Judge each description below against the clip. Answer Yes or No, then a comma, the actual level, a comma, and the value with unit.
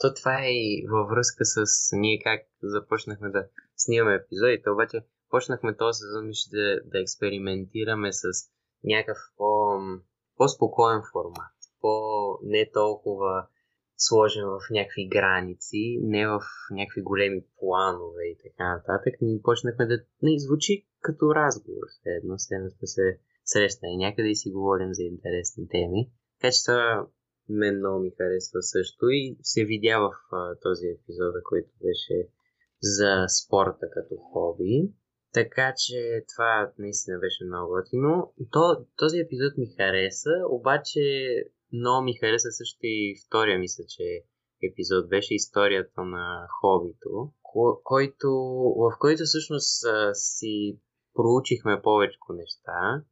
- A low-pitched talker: Yes, low, 110 Hz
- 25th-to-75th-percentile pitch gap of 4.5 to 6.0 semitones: Yes, wide, 5.4 semitones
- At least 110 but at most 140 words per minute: Yes, average, 125 wpm